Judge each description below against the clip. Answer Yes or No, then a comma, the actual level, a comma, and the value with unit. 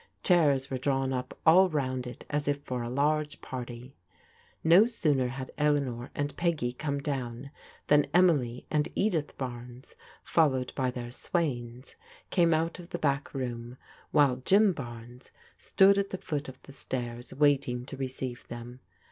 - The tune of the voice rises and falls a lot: No, average, 3.6 semitones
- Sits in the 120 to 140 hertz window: Yes, low, 135 Hz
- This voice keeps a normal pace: Yes, average, 155 wpm